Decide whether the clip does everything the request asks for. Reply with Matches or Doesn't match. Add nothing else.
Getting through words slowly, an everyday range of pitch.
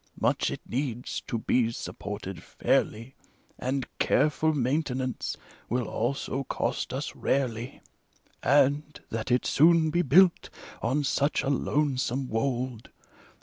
Matches